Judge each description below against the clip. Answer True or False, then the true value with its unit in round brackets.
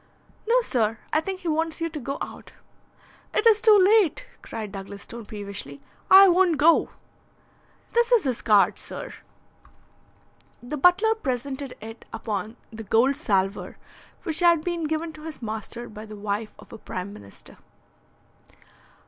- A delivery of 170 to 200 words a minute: False (150 wpm)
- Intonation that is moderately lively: False (8.2 semitones)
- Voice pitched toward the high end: True (275 Hz)